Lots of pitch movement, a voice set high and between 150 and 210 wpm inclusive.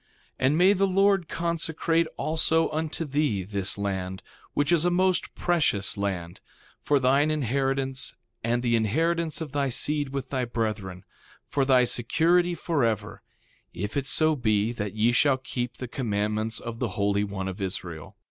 No: wide, 7.1 semitones; low, 130 Hz; average, 160 wpm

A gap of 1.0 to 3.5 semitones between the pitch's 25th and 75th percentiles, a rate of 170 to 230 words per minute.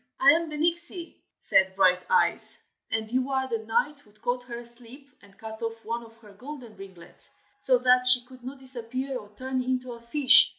Yes: average, 2.8 semitones; average, 195 wpm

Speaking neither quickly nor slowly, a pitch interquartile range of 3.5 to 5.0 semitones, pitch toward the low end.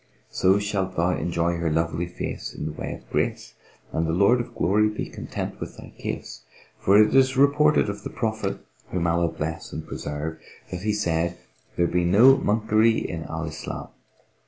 Yes: average, 180 wpm; average, 4.3 semitones; very low, 90 Hz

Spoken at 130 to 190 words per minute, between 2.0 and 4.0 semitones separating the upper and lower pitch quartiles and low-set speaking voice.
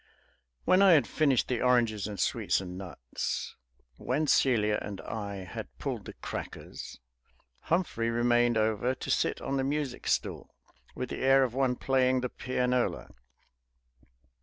Yes: average, 145 wpm; average, 3.7 semitones; low, 125 Hz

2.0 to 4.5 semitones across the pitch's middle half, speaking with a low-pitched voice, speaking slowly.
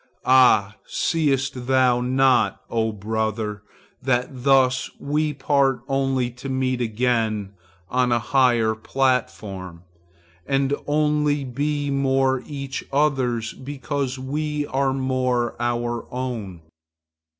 Yes: narrow, 2.5 semitones; low, 130 Hz; slow, 105 wpm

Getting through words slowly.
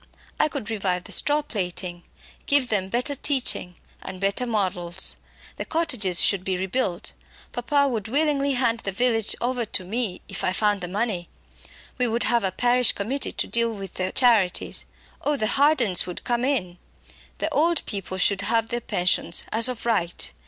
No: average, 175 wpm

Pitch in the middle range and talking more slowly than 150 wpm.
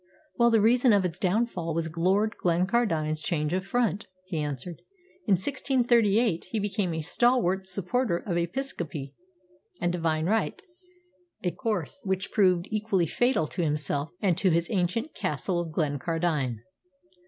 Yes: medium, 180 Hz; average, 140 wpm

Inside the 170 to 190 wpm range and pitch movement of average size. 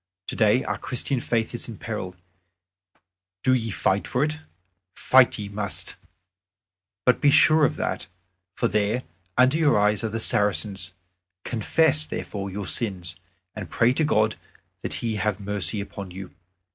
No: average, 145 wpm; average, 4.0 semitones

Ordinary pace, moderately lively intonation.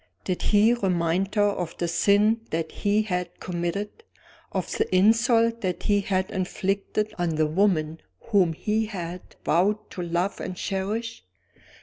Yes: average, 145 wpm; average, 3.3 semitones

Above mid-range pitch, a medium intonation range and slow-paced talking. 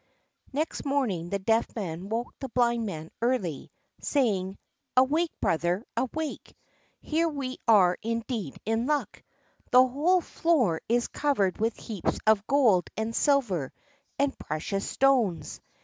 No: high, 230 Hz; wide, 5.9 semitones; slow, 130 wpm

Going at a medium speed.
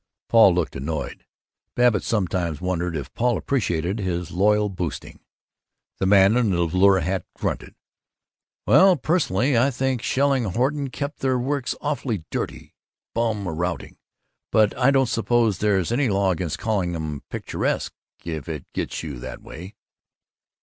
Yes: average, 145 wpm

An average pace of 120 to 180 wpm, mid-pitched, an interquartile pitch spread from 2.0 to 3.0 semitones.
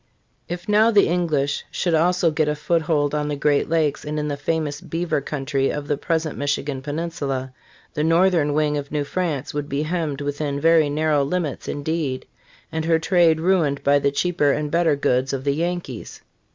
No: average, 190 wpm; medium, 150 Hz; narrow, 2.6 semitones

